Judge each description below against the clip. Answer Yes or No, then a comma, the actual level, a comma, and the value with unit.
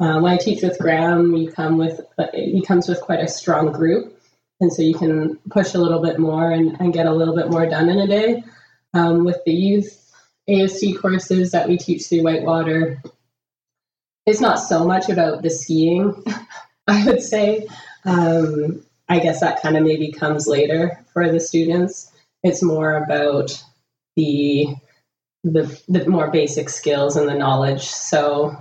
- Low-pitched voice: No, medium, 165 Hz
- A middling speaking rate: Yes, average, 170 wpm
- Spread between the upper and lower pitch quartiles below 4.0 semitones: Yes, narrow, 2.4 semitones